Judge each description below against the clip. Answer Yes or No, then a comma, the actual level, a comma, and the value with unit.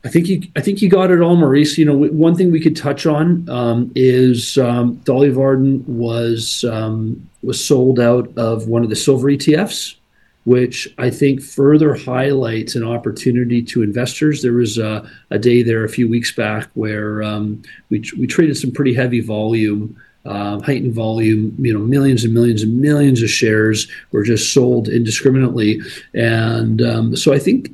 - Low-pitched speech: Yes, low, 120 Hz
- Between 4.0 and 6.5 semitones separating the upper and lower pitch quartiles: No, average, 3.6 semitones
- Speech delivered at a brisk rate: No, average, 175 wpm